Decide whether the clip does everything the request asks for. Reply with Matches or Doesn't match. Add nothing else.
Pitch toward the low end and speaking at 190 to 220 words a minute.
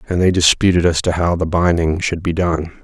Doesn't match